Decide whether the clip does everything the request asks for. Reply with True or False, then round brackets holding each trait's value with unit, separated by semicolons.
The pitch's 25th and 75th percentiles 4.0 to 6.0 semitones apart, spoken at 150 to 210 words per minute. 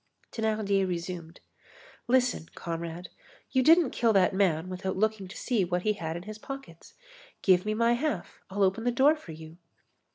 True (4.8 semitones; 170 wpm)